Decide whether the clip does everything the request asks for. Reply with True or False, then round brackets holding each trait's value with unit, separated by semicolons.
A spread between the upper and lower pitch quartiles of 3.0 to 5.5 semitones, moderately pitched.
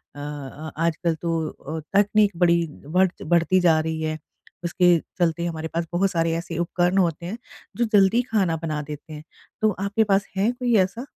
True (3.3 semitones; 170 Hz)